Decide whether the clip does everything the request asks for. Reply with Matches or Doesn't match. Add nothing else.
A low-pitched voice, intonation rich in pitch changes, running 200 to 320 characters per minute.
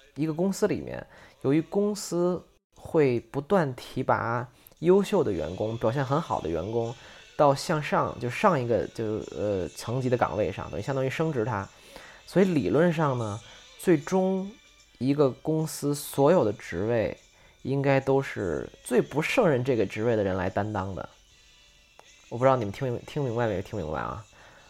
Matches